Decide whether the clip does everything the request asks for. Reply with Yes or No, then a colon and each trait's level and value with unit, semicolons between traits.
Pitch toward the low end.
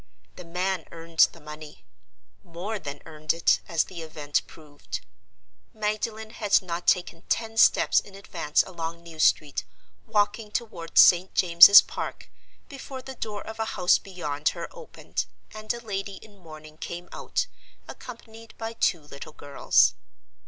No: medium, 175 Hz